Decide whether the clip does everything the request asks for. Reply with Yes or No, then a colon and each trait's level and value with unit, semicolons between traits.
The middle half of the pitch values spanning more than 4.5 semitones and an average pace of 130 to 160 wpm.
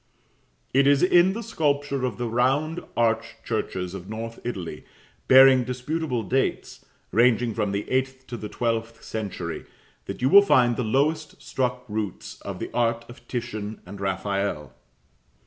No: average, 3.6 semitones; average, 150 wpm